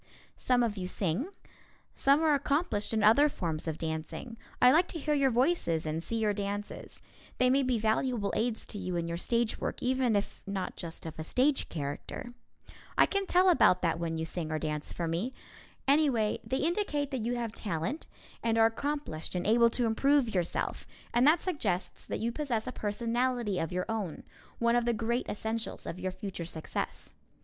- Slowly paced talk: No, average, 190 wpm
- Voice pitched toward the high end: Yes, high, 225 Hz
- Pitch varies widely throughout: Yes, wide, 6.1 semitones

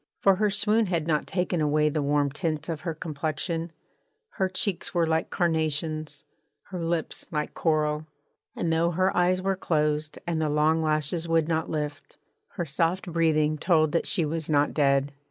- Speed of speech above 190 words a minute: No, average, 170 wpm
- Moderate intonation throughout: No, narrow, 2.3 semitones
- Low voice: No, medium, 160 Hz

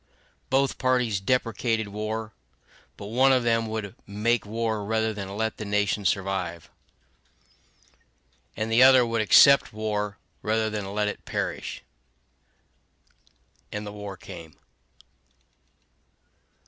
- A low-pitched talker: Yes, low, 110 Hz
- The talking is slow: Yes, slow, 115 wpm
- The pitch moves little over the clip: Yes, narrow, 2.0 semitones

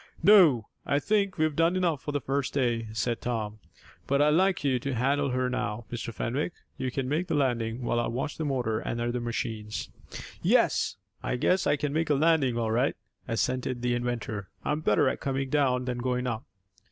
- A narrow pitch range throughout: No, average, 3.7 semitones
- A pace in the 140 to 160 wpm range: No, average, 200 wpm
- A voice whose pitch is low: Yes, low, 130 Hz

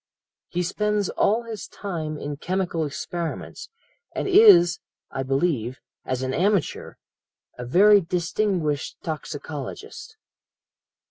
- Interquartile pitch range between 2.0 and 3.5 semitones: No, wide, 5.6 semitones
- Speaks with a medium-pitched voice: Yes, medium, 175 Hz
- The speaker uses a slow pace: Yes, slow, 105 wpm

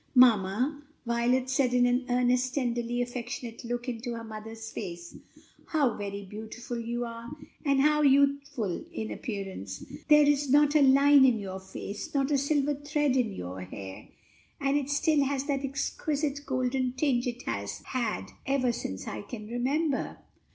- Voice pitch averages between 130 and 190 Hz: No, very high, 250 Hz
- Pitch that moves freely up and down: No, average, 3.9 semitones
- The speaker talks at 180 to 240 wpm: No, average, 160 wpm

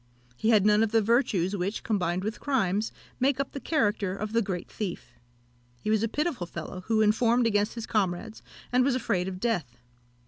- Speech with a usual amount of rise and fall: Yes, average, 3.6 semitones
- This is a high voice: Yes, high, 215 Hz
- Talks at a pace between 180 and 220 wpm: Yes, average, 195 wpm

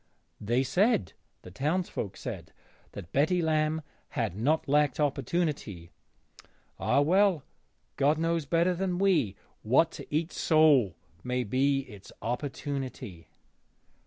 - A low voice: No, medium, 145 Hz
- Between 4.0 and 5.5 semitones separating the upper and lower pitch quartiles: Yes, average, 4.8 semitones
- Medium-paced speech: No, slow, 115 wpm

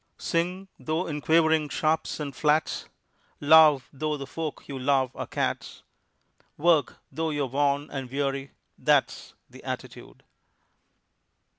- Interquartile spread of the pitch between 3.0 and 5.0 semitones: No, narrow, 2.4 semitones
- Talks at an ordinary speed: No, slow, 125 wpm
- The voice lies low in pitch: No, medium, 150 Hz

